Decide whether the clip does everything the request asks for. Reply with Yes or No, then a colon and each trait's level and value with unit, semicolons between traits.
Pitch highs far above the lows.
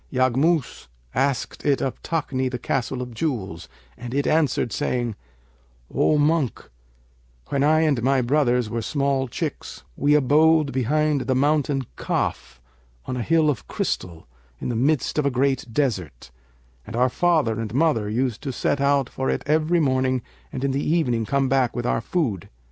No: average, 3.5 semitones